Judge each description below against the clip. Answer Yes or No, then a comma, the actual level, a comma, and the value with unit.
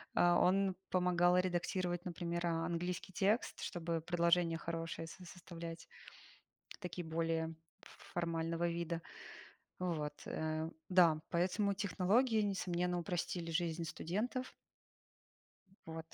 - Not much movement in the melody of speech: Yes, narrow, 1.7 semitones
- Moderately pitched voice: Yes, medium, 175 Hz